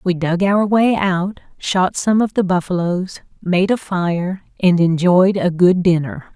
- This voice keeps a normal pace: Yes, average, 170 wpm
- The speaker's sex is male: No, female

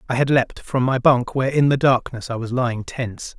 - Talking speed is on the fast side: Yes, fast, 250 wpm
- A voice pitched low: Yes, low, 125 Hz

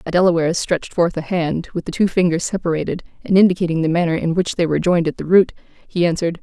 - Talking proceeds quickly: Yes, fast, 235 wpm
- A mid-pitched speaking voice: Yes, medium, 170 Hz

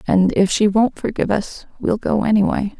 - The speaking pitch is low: No, high, 205 Hz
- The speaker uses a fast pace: No, average, 195 wpm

